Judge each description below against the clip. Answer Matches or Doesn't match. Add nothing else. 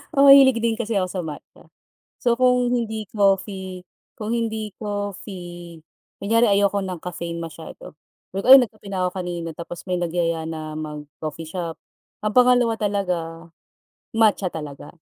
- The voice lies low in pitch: Doesn't match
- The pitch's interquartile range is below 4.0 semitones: Doesn't match